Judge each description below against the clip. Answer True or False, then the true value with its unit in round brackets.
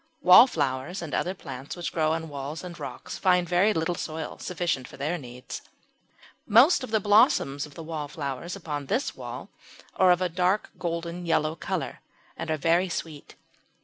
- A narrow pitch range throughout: False (3.5 semitones)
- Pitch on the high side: False (165 Hz)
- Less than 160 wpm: False (165 wpm)